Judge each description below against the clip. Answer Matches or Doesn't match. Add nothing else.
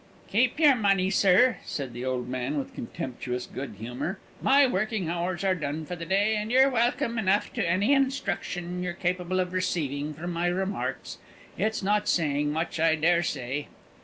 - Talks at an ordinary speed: Matches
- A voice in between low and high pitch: Matches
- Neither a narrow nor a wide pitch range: Doesn't match